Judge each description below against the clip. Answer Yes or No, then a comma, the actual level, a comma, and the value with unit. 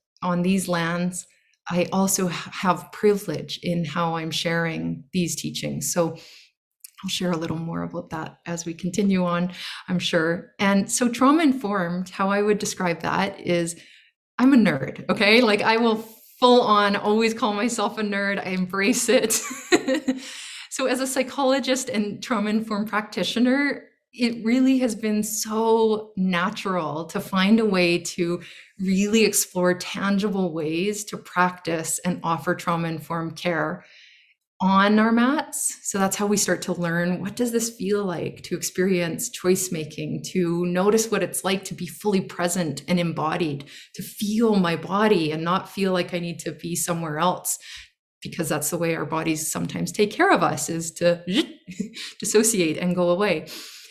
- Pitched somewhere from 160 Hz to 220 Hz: Yes, high, 190 Hz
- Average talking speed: Yes, average, 160 wpm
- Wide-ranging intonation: No, average, 3.8 semitones